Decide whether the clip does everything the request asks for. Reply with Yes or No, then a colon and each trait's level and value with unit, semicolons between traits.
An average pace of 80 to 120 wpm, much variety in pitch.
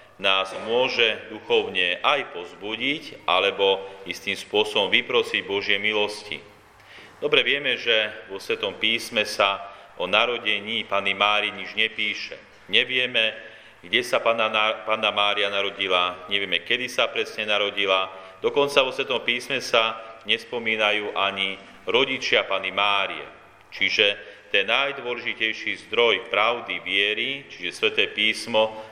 Yes: slow, 110 wpm; wide, 5.9 semitones